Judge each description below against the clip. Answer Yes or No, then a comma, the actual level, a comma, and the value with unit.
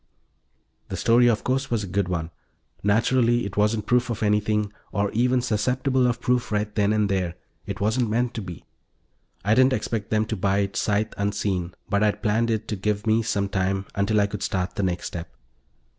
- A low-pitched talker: Yes, low, 105 Hz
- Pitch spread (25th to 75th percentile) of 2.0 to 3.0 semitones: Yes, average, 2.7 semitones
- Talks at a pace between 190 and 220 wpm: Yes, average, 200 wpm